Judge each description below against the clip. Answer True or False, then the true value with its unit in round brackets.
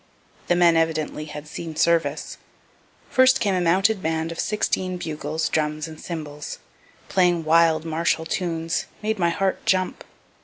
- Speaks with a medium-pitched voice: True (165 Hz)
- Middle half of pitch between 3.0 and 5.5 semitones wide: False (2.4 semitones)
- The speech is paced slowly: False (145 wpm)